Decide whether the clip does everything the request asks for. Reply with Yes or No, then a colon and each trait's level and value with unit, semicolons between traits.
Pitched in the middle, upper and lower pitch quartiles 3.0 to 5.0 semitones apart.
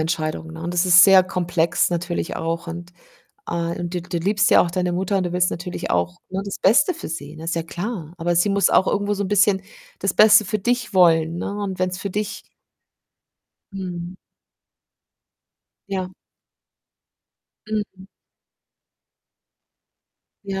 No: medium, 180 Hz; narrow, 2.5 semitones